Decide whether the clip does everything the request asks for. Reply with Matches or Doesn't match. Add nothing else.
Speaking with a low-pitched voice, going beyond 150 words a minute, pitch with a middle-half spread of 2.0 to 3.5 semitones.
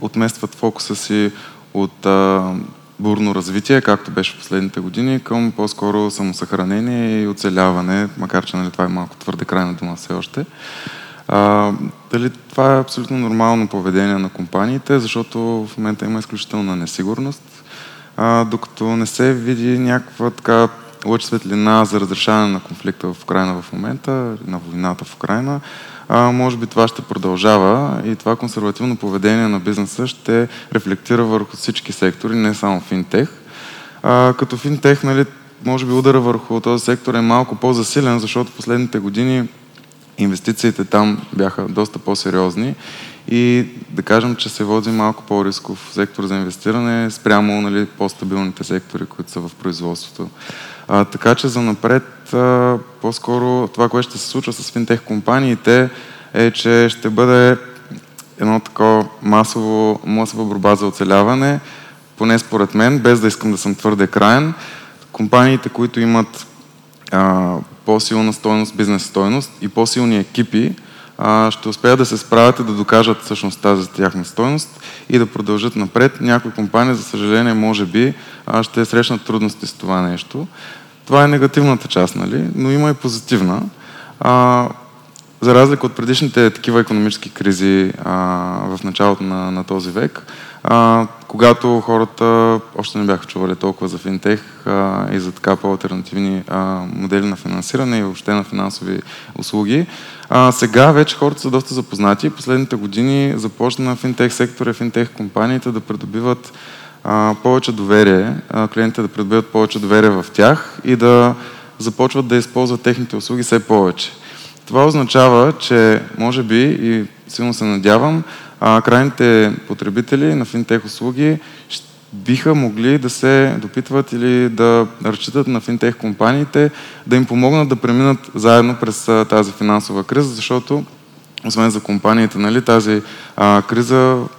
Doesn't match